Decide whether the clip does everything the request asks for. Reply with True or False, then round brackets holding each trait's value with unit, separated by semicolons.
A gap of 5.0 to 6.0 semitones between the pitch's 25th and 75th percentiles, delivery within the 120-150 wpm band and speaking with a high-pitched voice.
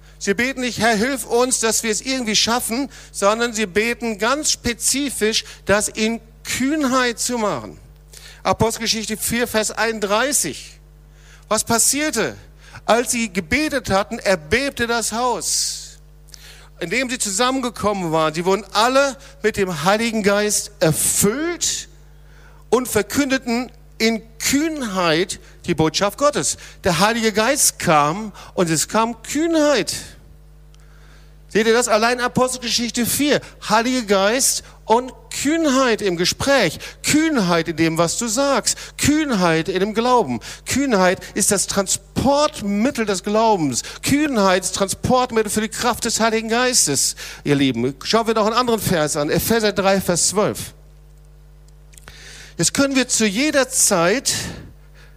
True (5.3 semitones; 130 wpm; 220 Hz)